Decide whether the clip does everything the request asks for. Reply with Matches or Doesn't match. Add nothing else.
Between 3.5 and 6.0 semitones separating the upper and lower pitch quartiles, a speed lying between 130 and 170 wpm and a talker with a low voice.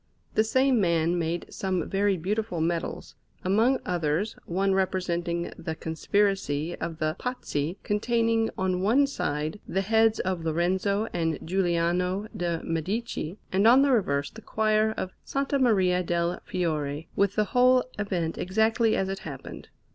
Doesn't match